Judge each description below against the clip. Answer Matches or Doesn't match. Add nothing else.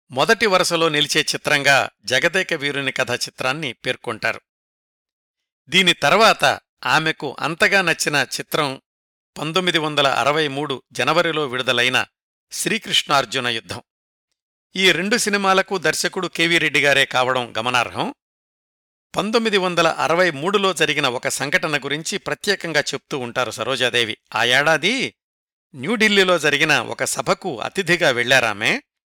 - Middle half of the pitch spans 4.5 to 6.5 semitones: Matches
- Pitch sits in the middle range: Matches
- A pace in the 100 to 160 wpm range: Matches